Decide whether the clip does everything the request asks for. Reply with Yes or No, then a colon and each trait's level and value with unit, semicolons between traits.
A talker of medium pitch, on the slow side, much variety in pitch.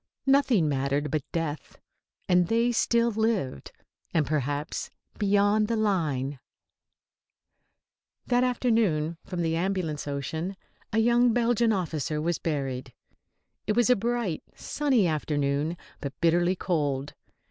Yes: medium, 175 Hz; slow, 115 wpm; wide, 7.1 semitones